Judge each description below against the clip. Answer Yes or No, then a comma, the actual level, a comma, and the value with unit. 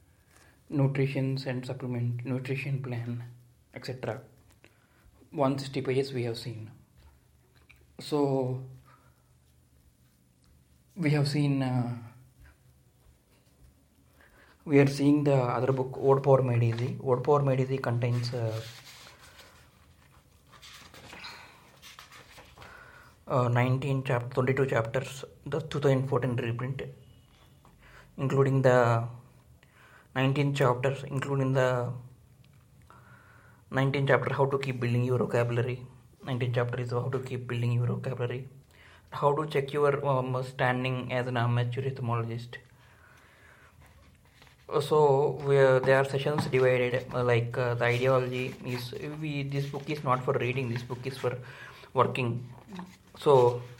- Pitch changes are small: Yes, narrow, 2.0 semitones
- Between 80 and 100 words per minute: No, average, 110 wpm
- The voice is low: Yes, low, 125 Hz